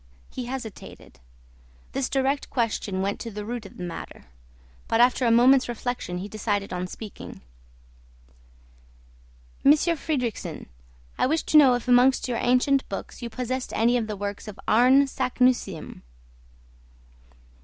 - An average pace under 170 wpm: Yes, average, 140 wpm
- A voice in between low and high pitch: No, high, 240 Hz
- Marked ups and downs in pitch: No, average, 3.8 semitones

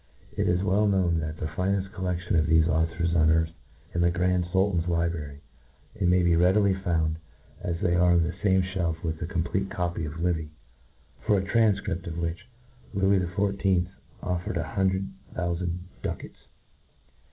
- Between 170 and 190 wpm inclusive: Yes, average, 175 wpm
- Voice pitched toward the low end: Yes, very low, 90 Hz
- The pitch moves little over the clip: Yes, narrow, 2.2 semitones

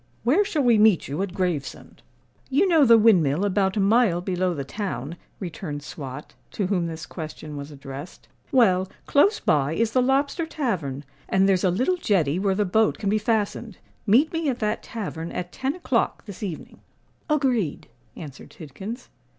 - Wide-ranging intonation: Yes, wide, 6.5 semitones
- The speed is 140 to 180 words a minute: Yes, average, 175 wpm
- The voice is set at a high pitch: Yes, high, 195 Hz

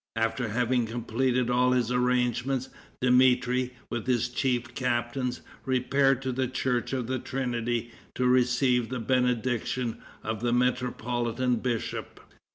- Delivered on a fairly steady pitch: Yes, narrow, 1.2 semitones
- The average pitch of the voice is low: Yes, low, 125 Hz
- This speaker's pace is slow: Yes, slow, 125 wpm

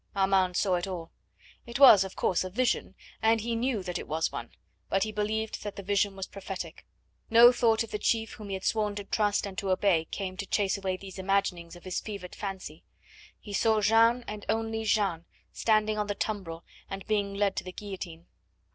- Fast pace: Yes, fast, 210 wpm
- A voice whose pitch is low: No, high, 200 Hz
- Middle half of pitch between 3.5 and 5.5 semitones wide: No, narrow, 2.5 semitones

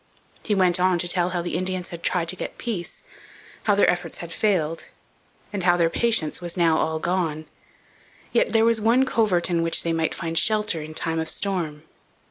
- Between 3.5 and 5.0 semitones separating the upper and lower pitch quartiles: No, average, 3.0 semitones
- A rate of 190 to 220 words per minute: Yes, average, 200 wpm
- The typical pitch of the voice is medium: Yes, medium, 175 Hz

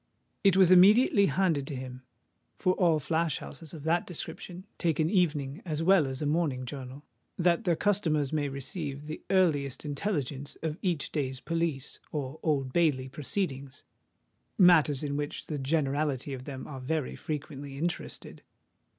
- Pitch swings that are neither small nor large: Yes, average, 3.8 semitones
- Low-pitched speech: No, medium, 150 Hz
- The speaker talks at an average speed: Yes, average, 150 wpm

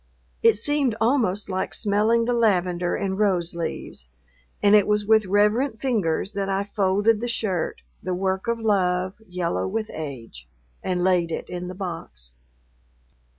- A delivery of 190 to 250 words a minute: No, average, 150 wpm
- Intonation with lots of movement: No, average, 3.4 semitones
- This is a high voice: Yes, high, 195 Hz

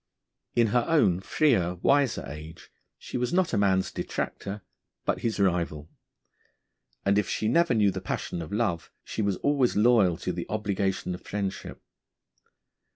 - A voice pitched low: Yes, low, 100 Hz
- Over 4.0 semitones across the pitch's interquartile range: Yes, average, 4.7 semitones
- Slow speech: No, average, 150 wpm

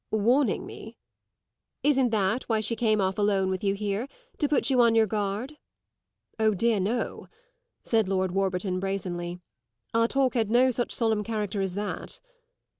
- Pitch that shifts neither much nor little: Yes, average, 3.3 semitones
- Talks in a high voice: Yes, high, 215 Hz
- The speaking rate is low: No, average, 160 wpm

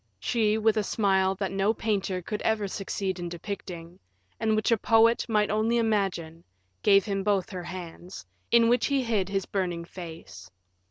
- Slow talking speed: No, average, 170 wpm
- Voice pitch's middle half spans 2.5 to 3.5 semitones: Yes, average, 3.0 semitones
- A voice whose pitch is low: No, high, 200 Hz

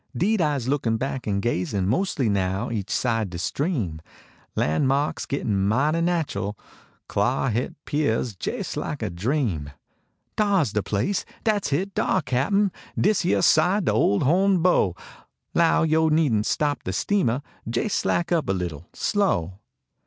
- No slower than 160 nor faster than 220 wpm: Yes, average, 175 wpm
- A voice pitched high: No, low, 135 Hz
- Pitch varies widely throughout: Yes, wide, 8.8 semitones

